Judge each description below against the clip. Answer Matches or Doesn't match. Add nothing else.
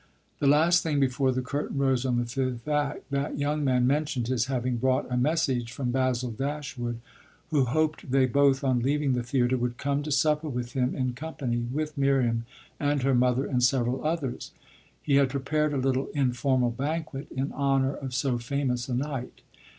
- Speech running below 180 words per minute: Doesn't match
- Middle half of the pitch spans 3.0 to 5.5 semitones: Doesn't match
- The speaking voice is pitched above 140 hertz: Doesn't match